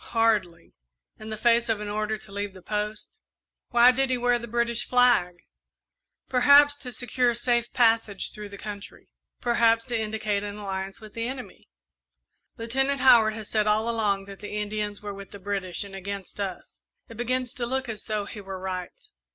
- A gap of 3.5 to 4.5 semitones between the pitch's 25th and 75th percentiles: No, average, 2.9 semitones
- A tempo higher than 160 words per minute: Yes, average, 185 wpm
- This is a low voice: No, high, 215 Hz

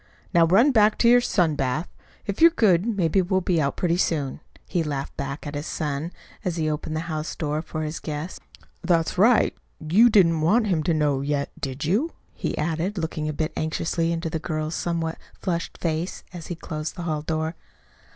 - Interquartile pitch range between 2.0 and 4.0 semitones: Yes, average, 2.8 semitones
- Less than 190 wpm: No, average, 200 wpm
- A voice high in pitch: No, medium, 165 Hz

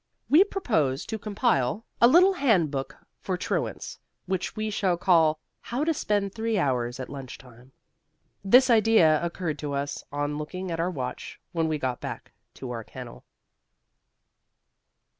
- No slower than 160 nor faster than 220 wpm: No, average, 150 wpm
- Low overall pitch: No, medium, 170 Hz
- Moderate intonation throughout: No, wide, 7.7 semitones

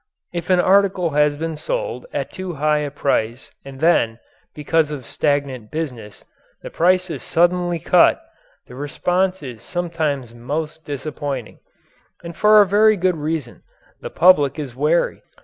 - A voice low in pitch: No, medium, 155 Hz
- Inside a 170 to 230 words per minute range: No, average, 150 wpm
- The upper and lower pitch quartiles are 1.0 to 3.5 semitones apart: No, average, 4.0 semitones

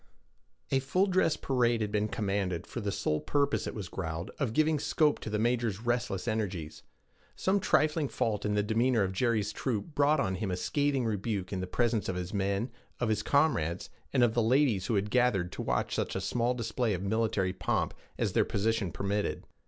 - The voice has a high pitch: No, low, 110 Hz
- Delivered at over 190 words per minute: Yes, average, 200 wpm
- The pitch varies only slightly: No, average, 4.2 semitones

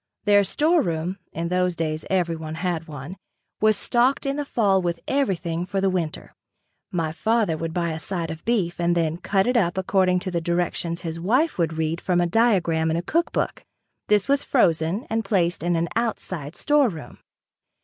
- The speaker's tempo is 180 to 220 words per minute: Yes, average, 185 wpm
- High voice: No, medium, 175 Hz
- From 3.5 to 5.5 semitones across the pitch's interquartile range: Yes, average, 3.8 semitones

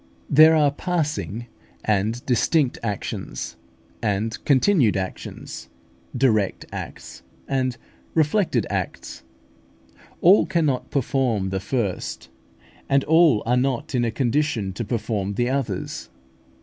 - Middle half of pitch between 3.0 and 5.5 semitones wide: Yes, average, 5.2 semitones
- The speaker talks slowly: Yes, slow, 110 wpm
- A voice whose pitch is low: Yes, low, 125 Hz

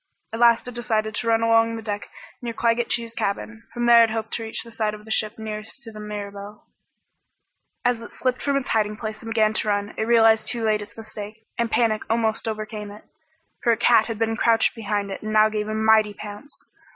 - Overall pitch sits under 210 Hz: No, high, 220 Hz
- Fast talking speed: Yes, fast, 225 wpm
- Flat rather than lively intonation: Yes, narrow, 1.4 semitones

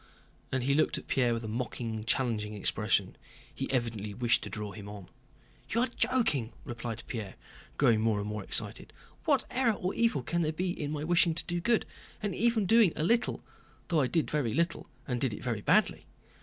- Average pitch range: No, wide, 7.7 semitones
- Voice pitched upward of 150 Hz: No, low, 125 Hz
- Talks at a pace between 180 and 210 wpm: Yes, average, 195 wpm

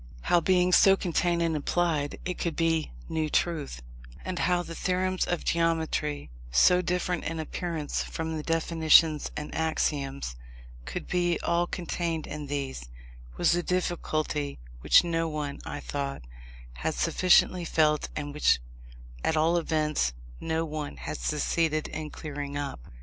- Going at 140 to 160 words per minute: Yes, average, 145 wpm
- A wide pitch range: No, average, 2.8 semitones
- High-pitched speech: No, medium, 160 Hz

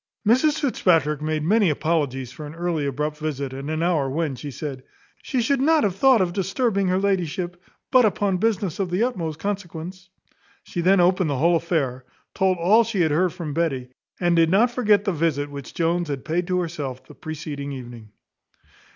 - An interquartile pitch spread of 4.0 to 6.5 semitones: Yes, average, 4.5 semitones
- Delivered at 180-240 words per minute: Yes, average, 190 wpm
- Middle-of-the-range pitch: Yes, medium, 170 Hz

